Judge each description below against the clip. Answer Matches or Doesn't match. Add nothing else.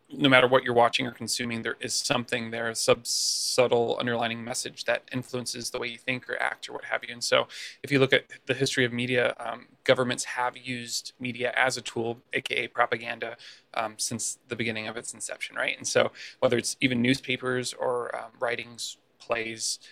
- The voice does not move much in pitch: Matches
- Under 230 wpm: Matches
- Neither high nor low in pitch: Doesn't match